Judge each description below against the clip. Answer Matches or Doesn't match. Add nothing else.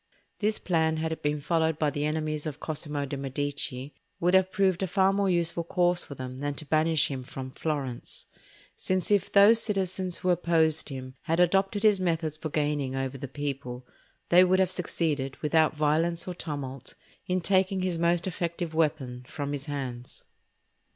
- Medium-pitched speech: Matches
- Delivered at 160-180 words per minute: Matches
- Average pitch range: Matches